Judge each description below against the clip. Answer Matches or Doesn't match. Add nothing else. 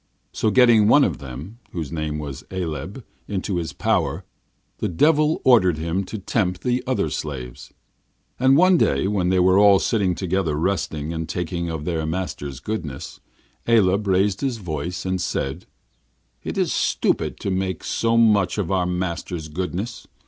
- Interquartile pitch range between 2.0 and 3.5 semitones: Doesn't match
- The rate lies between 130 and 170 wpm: Matches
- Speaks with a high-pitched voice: Doesn't match